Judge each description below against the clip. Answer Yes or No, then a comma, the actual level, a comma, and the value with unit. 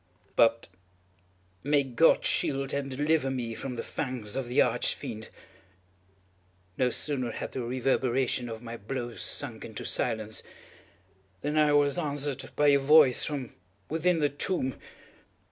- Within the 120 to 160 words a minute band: Yes, average, 140 wpm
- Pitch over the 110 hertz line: Yes, low, 135 Hz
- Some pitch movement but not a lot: Yes, average, 3.2 semitones